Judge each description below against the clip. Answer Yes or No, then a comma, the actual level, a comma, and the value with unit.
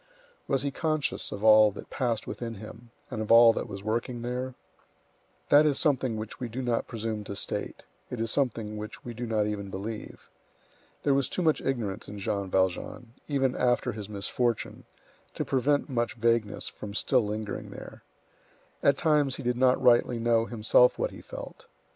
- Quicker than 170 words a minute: Yes, average, 180 wpm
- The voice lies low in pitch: Yes, low, 115 Hz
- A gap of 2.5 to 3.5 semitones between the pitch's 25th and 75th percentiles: Yes, average, 3.1 semitones